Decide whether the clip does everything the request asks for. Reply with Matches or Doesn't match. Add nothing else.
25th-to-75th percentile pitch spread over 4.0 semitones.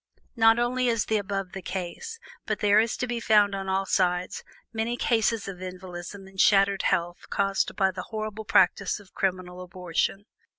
Doesn't match